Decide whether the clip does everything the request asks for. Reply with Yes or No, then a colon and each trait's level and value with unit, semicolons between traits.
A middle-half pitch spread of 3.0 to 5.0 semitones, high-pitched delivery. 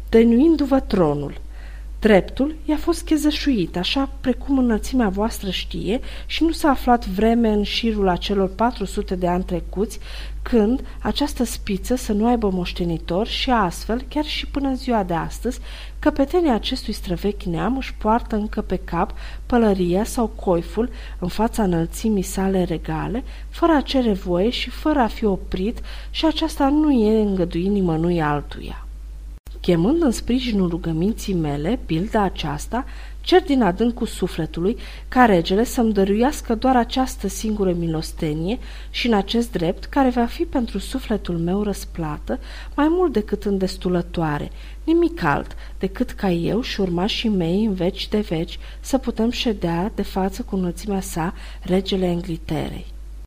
No: wide, 5.5 semitones; high, 210 Hz